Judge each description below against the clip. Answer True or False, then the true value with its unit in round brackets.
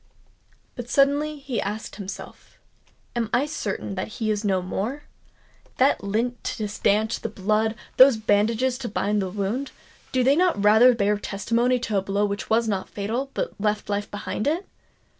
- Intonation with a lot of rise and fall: False (3.7 semitones)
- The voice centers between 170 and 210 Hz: False (220 Hz)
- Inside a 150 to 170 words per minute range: True (160 wpm)